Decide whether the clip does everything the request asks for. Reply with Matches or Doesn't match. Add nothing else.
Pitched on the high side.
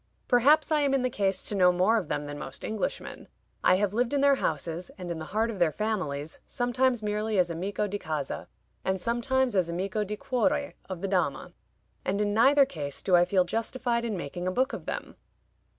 Matches